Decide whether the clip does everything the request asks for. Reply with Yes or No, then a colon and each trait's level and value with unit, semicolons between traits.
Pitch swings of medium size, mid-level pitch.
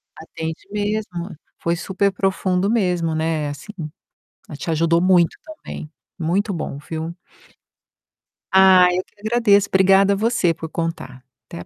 Yes: average, 3.4 semitones; medium, 180 Hz